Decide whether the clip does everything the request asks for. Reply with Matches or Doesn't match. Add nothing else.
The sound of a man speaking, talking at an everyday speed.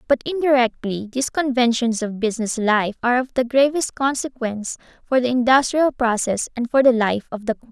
Doesn't match